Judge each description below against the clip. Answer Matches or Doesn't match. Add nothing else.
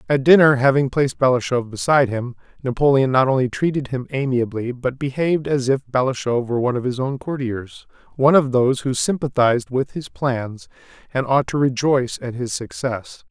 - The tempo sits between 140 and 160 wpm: Doesn't match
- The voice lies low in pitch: Matches